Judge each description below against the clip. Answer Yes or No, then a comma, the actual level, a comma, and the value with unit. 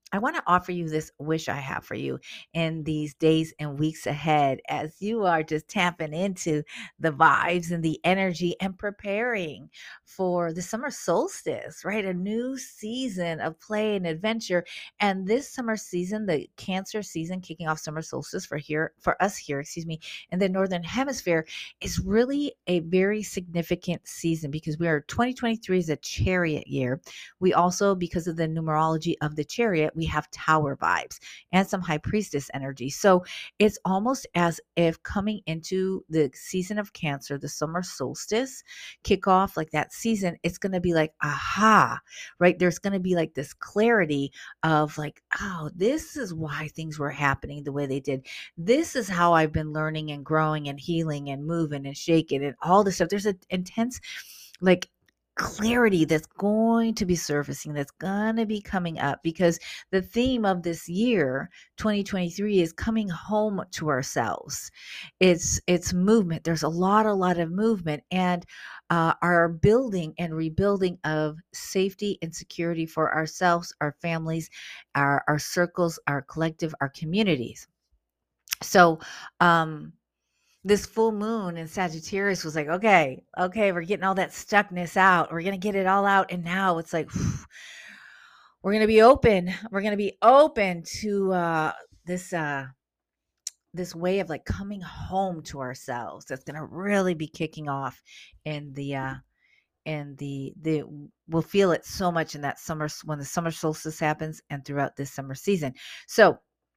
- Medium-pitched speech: Yes, medium, 170 Hz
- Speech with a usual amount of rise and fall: Yes, average, 4.2 semitones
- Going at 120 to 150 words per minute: No, average, 165 wpm